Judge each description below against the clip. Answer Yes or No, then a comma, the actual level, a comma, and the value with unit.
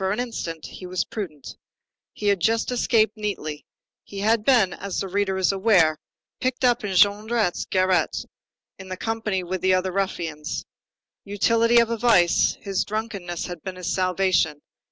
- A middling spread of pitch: Yes, average, 3.3 semitones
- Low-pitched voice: No, high, 195 Hz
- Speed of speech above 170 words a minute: No, average, 165 wpm